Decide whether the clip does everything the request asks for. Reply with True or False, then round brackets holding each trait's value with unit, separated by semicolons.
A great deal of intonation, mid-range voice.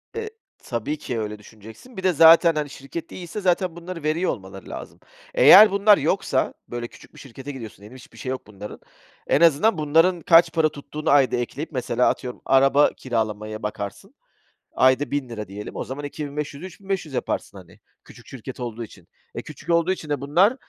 True (6.0 semitones; 145 Hz)